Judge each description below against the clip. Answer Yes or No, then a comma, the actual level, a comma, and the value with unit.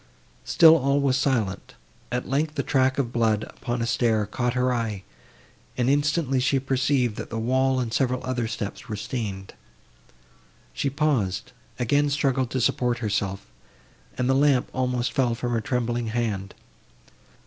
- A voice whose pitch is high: No, low, 125 Hz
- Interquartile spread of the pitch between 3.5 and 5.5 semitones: No, average, 2.7 semitones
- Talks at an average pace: Yes, average, 155 wpm